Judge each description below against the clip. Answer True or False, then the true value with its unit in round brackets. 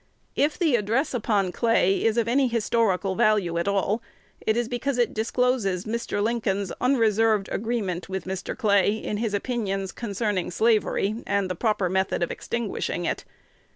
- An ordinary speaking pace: True (155 wpm)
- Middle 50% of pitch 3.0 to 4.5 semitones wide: True (3.3 semitones)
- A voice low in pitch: False (215 Hz)